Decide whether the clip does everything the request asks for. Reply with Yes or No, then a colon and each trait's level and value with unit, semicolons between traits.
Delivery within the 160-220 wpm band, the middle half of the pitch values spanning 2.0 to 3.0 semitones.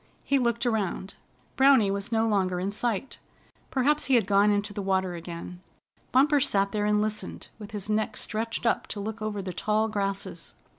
Yes: average, 185 wpm; narrow, 2.6 semitones